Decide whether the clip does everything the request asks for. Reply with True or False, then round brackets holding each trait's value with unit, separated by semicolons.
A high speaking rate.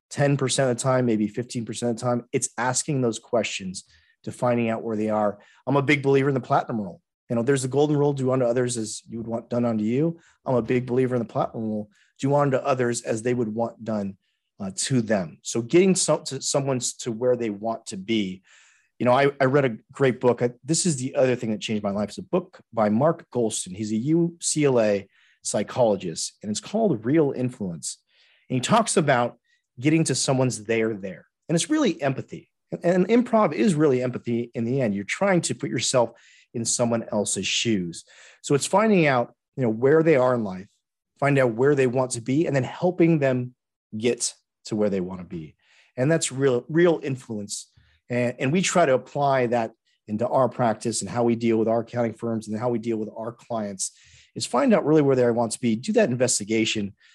True (215 wpm)